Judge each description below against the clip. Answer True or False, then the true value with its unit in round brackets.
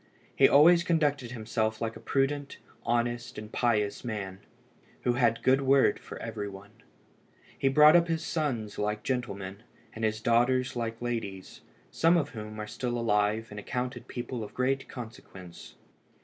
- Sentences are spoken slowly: False (160 wpm)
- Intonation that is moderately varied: True (3.7 semitones)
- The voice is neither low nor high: False (120 Hz)